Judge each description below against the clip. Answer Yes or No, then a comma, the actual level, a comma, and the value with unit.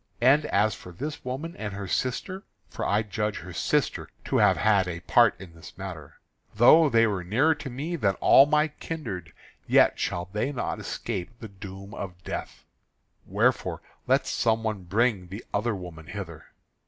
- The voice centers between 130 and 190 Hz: No, low, 105 Hz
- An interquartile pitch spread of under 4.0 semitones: No, average, 5.3 semitones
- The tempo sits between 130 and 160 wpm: No, average, 175 wpm